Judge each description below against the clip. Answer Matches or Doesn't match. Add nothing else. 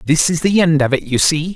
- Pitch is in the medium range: Matches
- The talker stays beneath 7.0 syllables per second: Matches